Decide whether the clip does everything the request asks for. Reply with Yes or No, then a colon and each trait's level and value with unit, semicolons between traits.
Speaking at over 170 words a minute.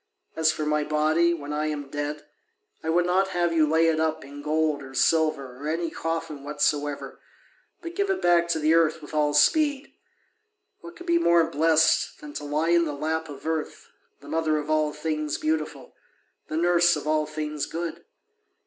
Yes: average, 190 wpm